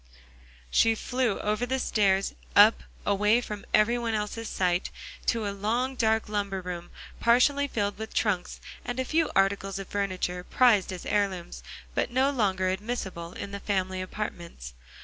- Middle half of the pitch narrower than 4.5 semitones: Yes, average, 3.5 semitones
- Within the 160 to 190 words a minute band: No, average, 150 wpm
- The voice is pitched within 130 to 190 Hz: No, high, 205 Hz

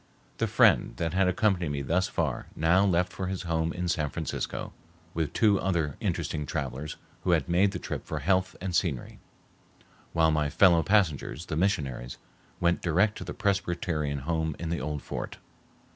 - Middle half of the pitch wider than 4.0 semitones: No, average, 3.4 semitones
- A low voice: Yes, very low, 85 Hz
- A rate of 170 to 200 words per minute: Yes, average, 175 wpm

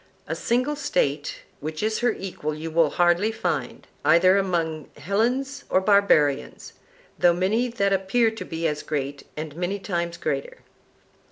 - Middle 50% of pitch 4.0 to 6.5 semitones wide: Yes, wide, 5.5 semitones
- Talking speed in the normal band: Yes, average, 150 wpm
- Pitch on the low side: No, medium, 185 Hz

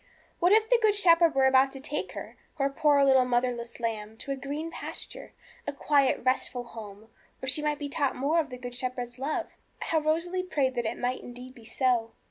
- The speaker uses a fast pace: Yes, fast, 210 wpm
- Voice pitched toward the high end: Yes, very high, 270 Hz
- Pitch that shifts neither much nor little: Yes, average, 3.6 semitones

